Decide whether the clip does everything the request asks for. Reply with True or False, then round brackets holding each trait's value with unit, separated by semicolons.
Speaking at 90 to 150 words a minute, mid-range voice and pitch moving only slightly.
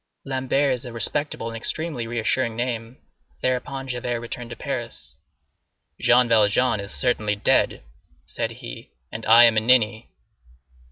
False (135 wpm; 120 Hz; 2.2 semitones)